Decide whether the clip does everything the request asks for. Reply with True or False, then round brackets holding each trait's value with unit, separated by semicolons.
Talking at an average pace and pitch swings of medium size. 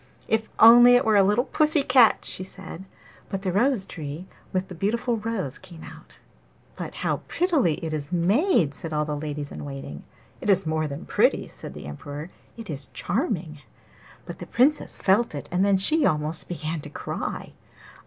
False (185 wpm; 6.8 semitones)